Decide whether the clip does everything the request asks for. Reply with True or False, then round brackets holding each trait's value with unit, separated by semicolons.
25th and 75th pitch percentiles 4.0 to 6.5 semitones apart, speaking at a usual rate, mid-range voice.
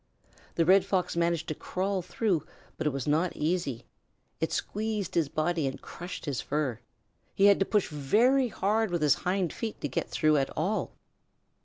True (4.6 semitones; 180 wpm; 175 Hz)